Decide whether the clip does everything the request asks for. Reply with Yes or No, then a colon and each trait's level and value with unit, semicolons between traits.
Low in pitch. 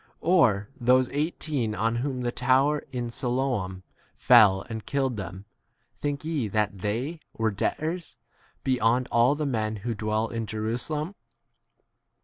Yes: low, 120 Hz